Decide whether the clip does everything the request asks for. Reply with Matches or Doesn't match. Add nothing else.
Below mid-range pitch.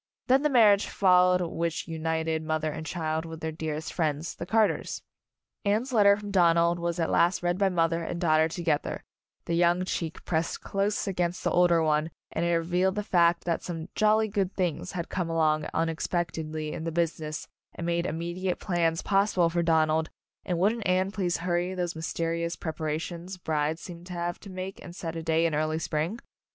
Doesn't match